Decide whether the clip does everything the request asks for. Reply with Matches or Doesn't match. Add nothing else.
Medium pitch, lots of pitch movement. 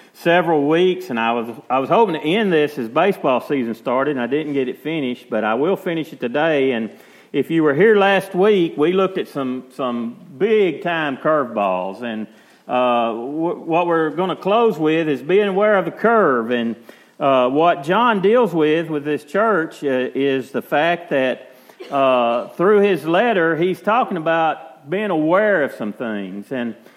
Matches